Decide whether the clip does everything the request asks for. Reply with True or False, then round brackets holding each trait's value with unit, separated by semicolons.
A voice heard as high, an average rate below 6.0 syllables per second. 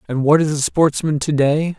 False (150 Hz; 4.7 syllables/s)